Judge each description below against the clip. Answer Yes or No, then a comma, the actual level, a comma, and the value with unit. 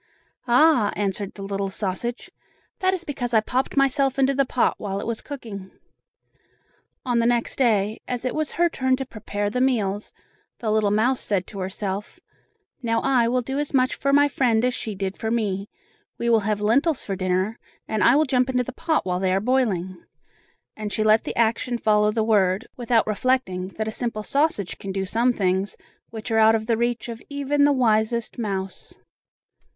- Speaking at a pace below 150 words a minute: No, average, 195 wpm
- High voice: Yes, high, 225 Hz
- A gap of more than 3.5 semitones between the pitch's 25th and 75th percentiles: Yes, average, 3.9 semitones